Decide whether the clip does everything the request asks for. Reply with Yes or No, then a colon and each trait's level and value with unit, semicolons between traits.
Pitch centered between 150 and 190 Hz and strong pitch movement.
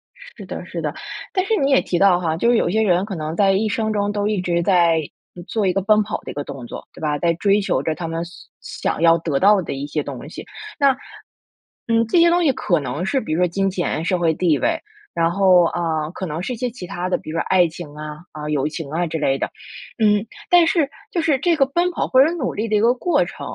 Yes: medium, 185 Hz; wide, 5.7 semitones